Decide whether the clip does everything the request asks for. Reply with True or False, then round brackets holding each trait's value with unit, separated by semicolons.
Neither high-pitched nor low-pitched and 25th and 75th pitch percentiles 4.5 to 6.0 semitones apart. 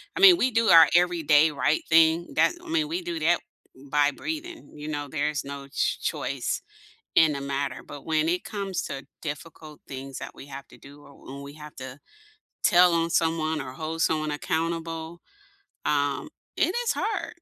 False (160 Hz; 3.2 semitones)